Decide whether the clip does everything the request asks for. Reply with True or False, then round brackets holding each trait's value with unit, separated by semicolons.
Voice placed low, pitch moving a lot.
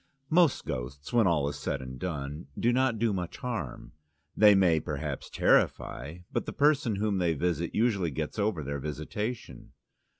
True (90 Hz; 7.2 semitones)